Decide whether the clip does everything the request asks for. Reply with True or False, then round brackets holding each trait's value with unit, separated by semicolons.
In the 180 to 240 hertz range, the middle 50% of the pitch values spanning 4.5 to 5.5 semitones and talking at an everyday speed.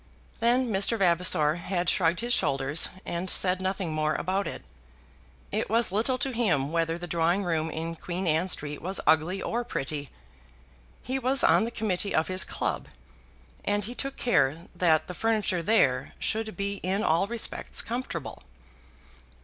True (185 Hz; 5.1 semitones; 160 wpm)